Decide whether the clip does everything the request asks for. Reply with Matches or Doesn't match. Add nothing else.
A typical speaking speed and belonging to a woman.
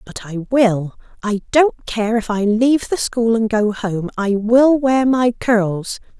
Matches